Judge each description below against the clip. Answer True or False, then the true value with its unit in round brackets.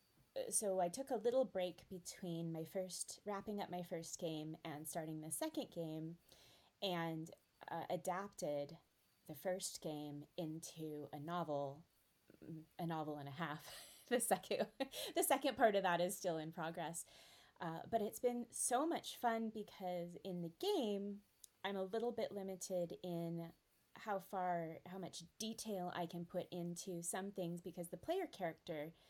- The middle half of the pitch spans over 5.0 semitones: False (3.3 semitones)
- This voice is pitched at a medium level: True (180 Hz)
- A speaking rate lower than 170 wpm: True (155 wpm)